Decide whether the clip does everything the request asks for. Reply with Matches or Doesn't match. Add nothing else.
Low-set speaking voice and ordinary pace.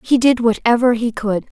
Doesn't match